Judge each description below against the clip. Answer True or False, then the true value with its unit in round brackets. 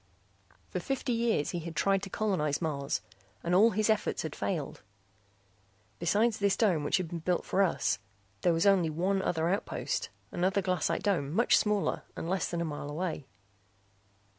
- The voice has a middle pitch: True (180 Hz)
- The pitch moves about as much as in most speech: True (3.7 semitones)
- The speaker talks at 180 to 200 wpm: False (170 wpm)